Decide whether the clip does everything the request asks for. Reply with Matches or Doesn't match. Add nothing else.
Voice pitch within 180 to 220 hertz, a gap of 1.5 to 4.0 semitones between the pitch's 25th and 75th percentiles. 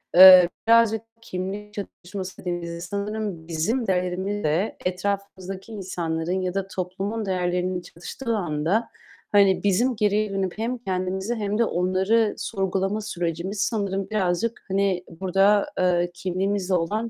Matches